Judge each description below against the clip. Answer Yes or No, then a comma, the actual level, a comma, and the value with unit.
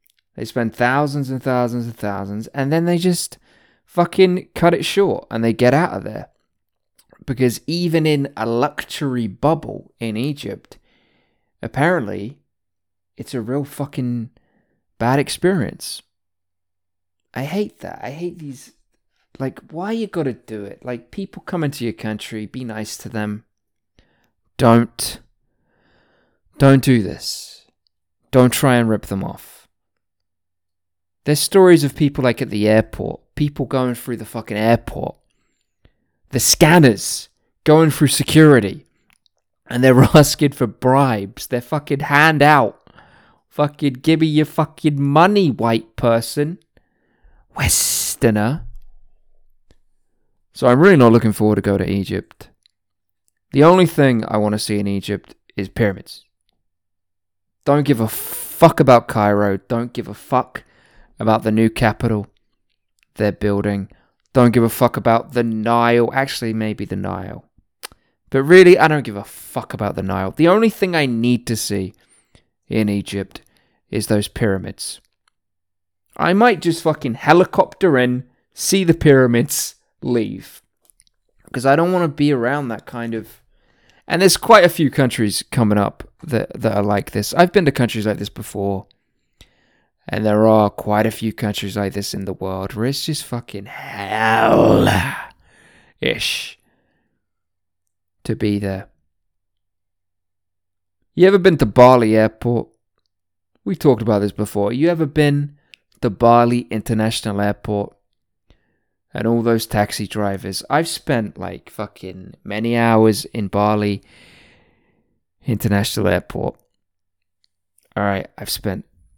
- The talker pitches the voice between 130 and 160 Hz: No, low, 115 Hz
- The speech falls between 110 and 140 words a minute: Yes, slow, 135 wpm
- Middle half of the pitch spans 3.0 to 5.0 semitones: No, wide, 5.6 semitones